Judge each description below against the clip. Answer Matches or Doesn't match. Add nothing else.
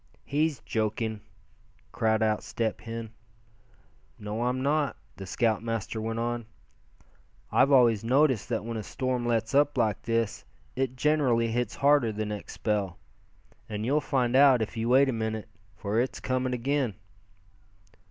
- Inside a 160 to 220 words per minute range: Doesn't match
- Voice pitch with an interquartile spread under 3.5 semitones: Matches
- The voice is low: Matches